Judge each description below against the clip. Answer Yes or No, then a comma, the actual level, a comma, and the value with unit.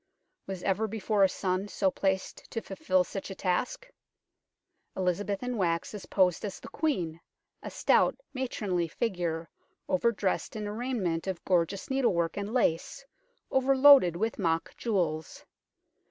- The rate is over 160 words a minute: No, average, 145 wpm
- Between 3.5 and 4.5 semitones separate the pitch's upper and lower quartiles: Yes, average, 4.1 semitones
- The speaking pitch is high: Yes, high, 195 Hz